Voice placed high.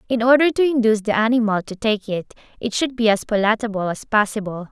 Yes: high, 220 Hz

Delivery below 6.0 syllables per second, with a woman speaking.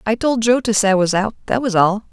No: 6.1 syllables/s; female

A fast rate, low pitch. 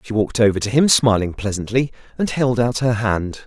Yes: fast, 210 wpm; low, 115 Hz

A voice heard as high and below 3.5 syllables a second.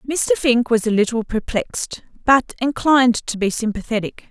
No: high, 240 Hz; 5.1 syllables/s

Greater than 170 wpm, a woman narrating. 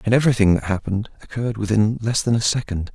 No: fast, 205 wpm; male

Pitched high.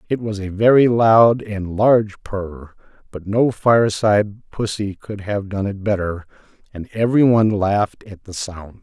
No: low, 105 Hz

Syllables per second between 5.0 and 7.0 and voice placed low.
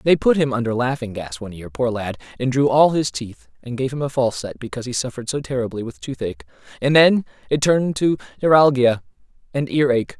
Yes: 6.2 syllables/s; low, 125 Hz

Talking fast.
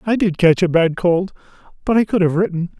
Yes: fast, 215 wpm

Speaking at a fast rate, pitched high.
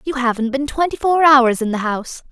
Yes: fast, 235 wpm; very high, 260 Hz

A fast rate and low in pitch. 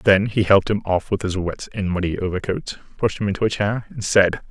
Yes: fast, 240 wpm; low, 100 Hz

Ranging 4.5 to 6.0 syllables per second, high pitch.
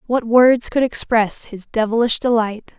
No: 4.3 syllables/s; high, 230 Hz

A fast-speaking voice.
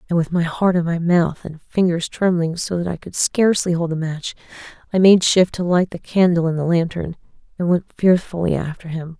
Yes: fast, 215 wpm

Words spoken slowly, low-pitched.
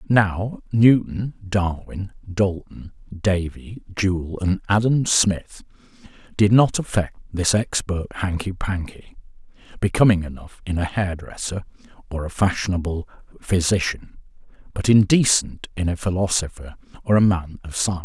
Yes: slow, 115 wpm; very low, 95 Hz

